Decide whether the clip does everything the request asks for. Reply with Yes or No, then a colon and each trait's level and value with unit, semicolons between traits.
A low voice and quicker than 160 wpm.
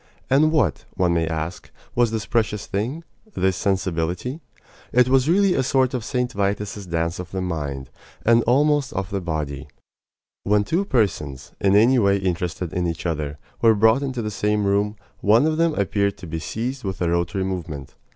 Yes: low, 100 Hz; average, 180 wpm